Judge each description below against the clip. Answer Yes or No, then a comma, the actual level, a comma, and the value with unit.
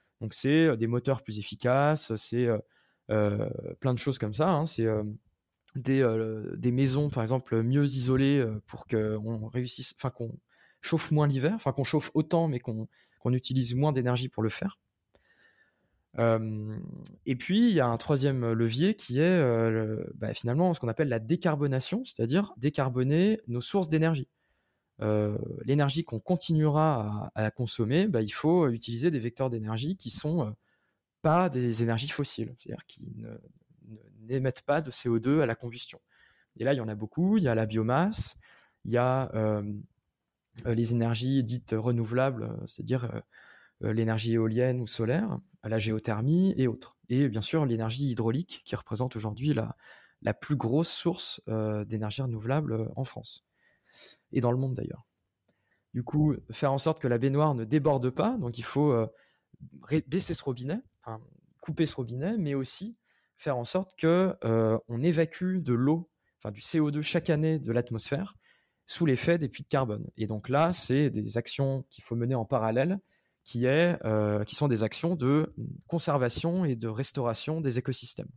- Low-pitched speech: Yes, low, 130 Hz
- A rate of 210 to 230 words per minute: No, average, 170 wpm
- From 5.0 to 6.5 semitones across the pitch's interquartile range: Yes, average, 5.3 semitones